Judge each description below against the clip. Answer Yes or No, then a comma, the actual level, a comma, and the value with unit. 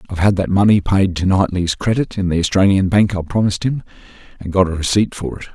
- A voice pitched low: Yes, very low, 95 Hz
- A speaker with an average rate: No, fast, 225 wpm